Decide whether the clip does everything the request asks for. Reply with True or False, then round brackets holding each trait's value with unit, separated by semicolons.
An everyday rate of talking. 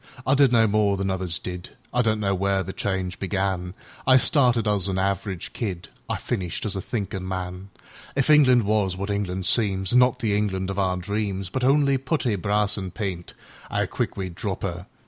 True (170 wpm)